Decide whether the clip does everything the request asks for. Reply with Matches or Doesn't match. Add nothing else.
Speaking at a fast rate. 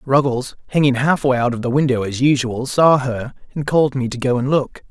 Matches